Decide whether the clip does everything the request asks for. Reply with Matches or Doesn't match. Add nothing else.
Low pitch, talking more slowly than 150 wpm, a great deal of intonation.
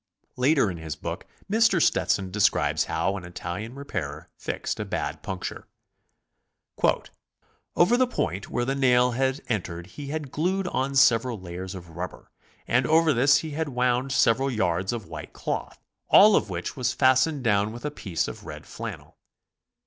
Doesn't match